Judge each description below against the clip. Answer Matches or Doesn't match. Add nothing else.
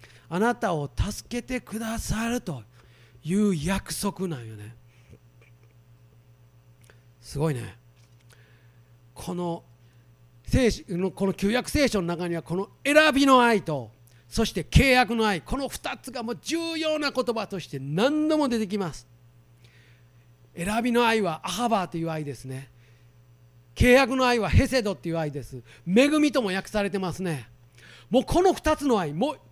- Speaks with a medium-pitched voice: Matches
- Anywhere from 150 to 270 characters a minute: Matches